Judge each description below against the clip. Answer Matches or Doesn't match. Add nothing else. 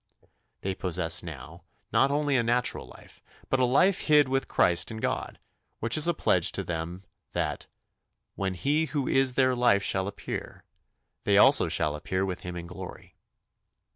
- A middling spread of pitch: Doesn't match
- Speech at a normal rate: Matches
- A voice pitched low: Matches